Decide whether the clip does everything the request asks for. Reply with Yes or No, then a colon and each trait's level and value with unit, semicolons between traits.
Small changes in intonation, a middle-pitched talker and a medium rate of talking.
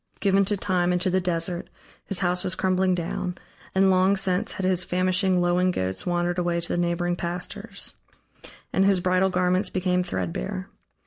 Yes: narrow, 1.2 semitones; medium, 180 Hz; average, 175 wpm